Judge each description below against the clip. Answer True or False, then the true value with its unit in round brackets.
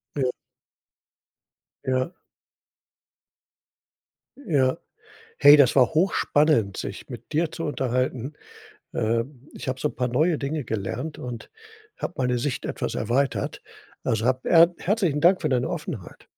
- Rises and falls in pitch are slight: False (3.8 semitones)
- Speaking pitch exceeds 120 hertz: True (135 Hz)